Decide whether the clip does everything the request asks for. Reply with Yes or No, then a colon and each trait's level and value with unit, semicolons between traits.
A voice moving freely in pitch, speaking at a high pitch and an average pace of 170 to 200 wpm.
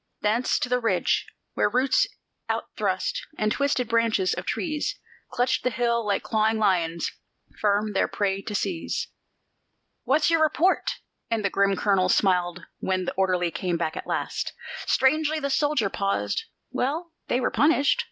No: wide, 6.2 semitones; high, 220 Hz; average, 155 wpm